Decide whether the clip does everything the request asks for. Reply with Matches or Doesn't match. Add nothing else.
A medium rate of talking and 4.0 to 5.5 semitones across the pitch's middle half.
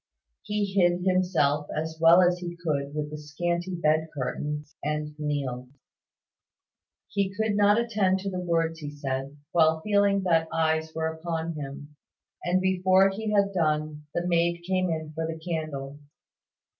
Doesn't match